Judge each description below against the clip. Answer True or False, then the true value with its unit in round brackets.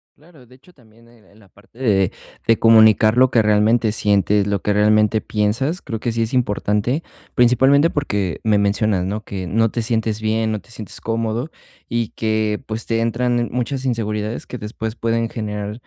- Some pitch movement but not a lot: False (2.2 semitones)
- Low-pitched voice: True (110 Hz)